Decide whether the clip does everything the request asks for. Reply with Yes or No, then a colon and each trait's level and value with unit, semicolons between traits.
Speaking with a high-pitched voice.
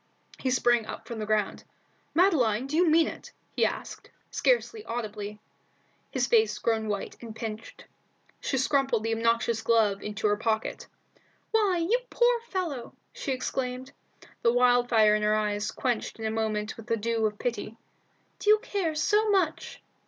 Yes: high, 230 Hz